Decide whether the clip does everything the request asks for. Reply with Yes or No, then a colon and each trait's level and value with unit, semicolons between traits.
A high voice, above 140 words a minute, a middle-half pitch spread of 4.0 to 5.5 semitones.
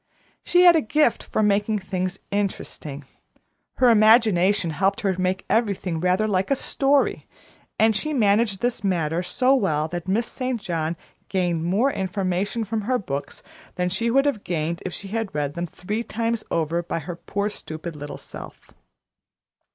Yes: high, 195 Hz; average, 165 wpm; average, 4.5 semitones